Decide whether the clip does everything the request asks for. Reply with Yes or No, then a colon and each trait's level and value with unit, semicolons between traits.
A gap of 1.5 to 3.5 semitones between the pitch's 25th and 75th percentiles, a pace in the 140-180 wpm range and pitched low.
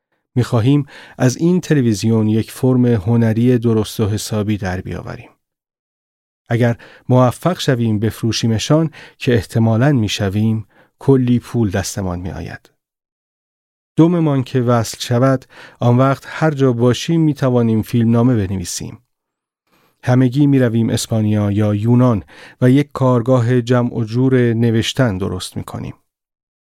No: average, 3.1 semitones; average, 120 wpm; low, 120 Hz